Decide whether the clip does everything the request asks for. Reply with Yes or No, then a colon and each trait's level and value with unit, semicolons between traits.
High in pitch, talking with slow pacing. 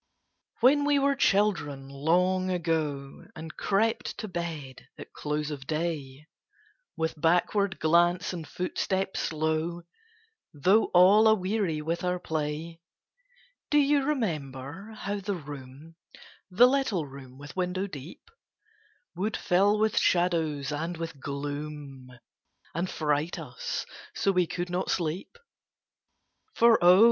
No: medium, 170 Hz; slow, 120 wpm